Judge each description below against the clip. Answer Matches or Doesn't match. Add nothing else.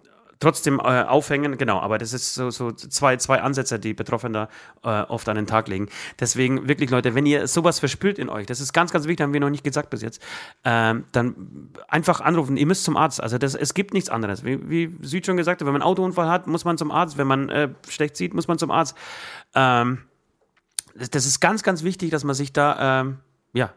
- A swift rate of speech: Matches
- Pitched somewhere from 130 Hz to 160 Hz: Matches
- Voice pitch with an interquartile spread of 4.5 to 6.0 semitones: Matches